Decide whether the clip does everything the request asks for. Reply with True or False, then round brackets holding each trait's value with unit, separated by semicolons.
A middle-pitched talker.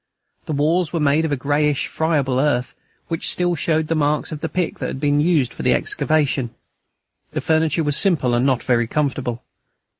True (150 Hz)